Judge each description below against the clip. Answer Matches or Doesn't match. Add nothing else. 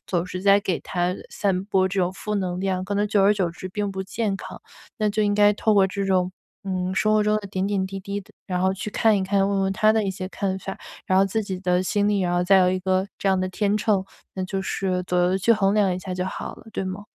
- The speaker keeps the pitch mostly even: Matches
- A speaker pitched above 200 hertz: Doesn't match